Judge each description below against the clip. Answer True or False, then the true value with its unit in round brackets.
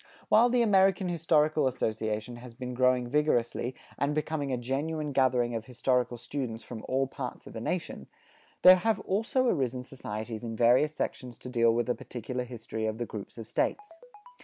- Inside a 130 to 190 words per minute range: True (175 wpm)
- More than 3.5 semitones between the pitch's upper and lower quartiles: True (4.4 semitones)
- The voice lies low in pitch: True (125 Hz)